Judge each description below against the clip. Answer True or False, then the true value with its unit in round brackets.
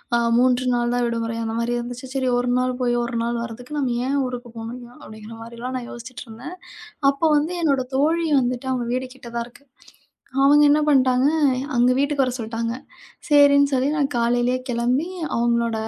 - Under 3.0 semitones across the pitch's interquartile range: True (2.4 semitones)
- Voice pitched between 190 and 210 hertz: False (245 Hz)